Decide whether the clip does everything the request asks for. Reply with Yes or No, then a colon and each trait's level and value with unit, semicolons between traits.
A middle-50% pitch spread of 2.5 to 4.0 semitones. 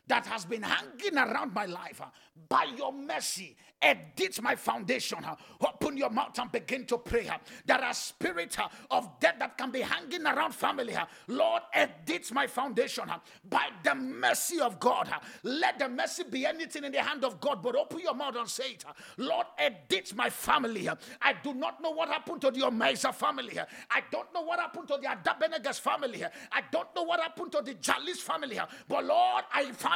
No: average, 4.5 semitones